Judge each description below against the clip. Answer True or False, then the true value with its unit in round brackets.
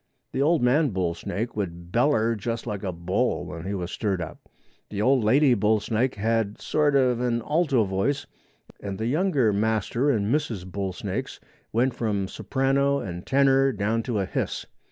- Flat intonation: False (5.1 semitones)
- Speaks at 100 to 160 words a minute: False (175 wpm)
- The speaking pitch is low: True (115 Hz)